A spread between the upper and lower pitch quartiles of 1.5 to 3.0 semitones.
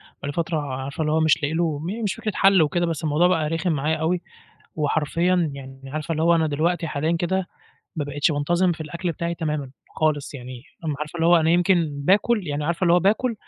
Yes: average, 2.7 semitones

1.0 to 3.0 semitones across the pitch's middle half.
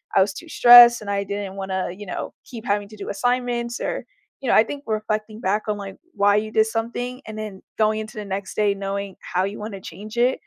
Yes: narrow, 2.4 semitones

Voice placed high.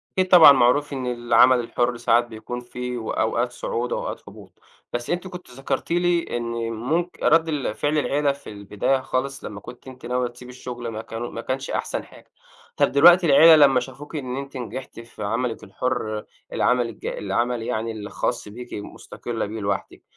No: low, 125 Hz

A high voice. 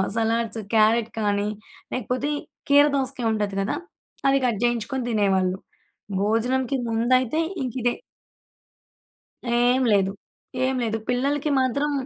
Yes: high, 235 Hz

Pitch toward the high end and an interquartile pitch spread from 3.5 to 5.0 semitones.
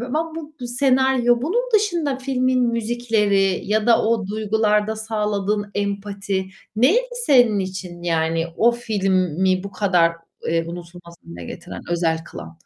Yes: high, 210 Hz; average, 4.7 semitones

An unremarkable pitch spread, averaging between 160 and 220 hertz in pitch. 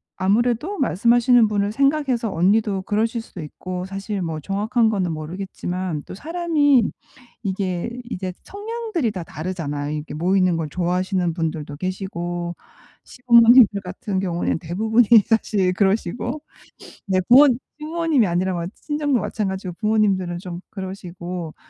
Yes: average, 4.8 semitones; high, 195 Hz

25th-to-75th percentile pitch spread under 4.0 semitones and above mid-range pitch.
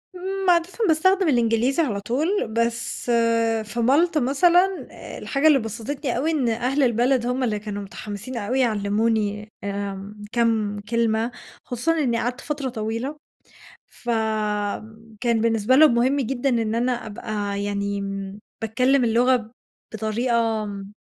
Yes: average, 3.6 semitones; high, 235 Hz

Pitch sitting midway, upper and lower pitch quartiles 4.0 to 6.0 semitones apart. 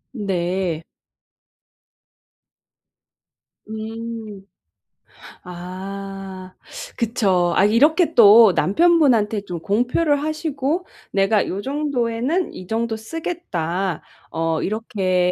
No: high, 215 Hz; wide, 5.5 semitones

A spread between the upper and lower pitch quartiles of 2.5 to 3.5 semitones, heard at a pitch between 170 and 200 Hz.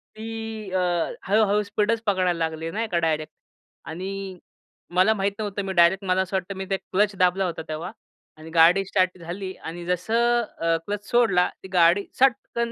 Yes: average, 3.0 semitones; high, 190 Hz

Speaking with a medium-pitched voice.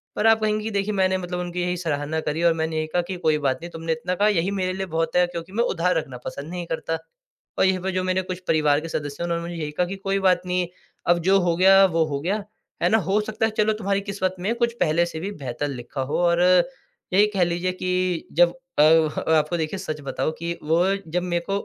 Yes: medium, 180 Hz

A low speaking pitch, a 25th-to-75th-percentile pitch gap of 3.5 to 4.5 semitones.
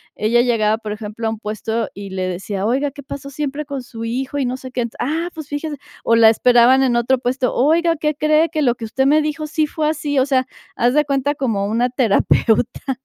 No: very high, 255 Hz; average, 4.2 semitones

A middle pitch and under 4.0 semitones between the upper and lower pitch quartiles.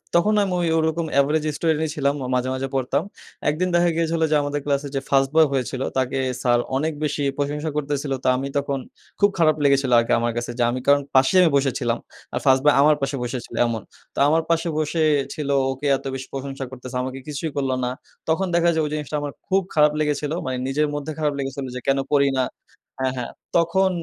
Yes: medium, 145 Hz; average, 2.9 semitones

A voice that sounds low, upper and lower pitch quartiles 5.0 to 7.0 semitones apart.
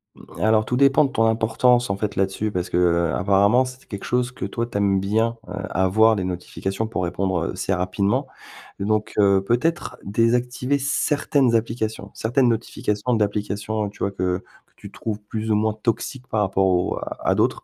No: low, 110 Hz; average, 3.4 semitones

